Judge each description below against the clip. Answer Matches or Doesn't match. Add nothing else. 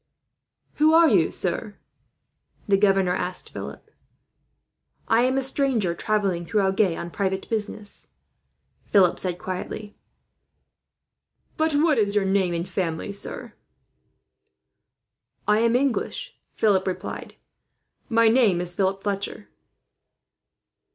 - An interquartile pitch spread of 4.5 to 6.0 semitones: Doesn't match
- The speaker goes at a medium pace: Doesn't match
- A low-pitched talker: Doesn't match